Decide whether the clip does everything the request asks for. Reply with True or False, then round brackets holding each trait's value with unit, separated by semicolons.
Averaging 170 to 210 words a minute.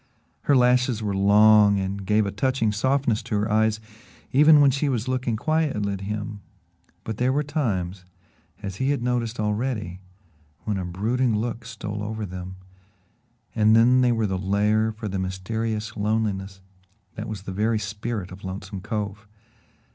False (160 wpm)